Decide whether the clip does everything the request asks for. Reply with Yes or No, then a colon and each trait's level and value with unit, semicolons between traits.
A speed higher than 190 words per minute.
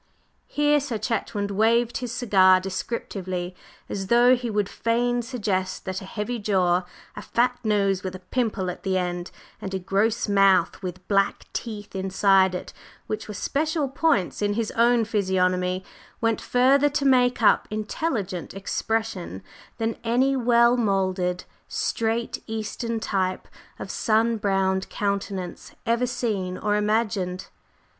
No: average, 140 wpm